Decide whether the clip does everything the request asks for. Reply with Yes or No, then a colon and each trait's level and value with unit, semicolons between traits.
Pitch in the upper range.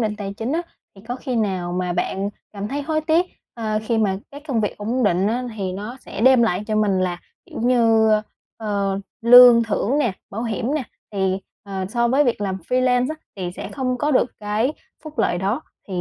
Yes: high, 220 Hz